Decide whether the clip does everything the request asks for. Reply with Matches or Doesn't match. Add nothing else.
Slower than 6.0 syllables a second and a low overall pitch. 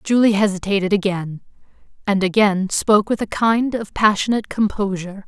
Doesn't match